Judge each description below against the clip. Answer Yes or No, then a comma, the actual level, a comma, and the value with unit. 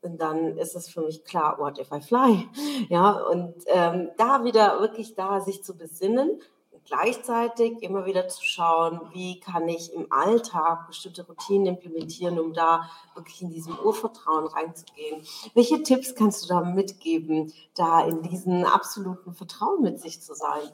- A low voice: No, medium, 180 Hz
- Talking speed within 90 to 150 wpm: No, average, 165 wpm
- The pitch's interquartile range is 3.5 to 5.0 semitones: Yes, average, 3.8 semitones